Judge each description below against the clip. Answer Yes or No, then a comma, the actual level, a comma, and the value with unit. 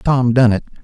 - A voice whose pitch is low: Yes, low, 120 Hz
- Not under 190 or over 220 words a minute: Yes, fast, 215 wpm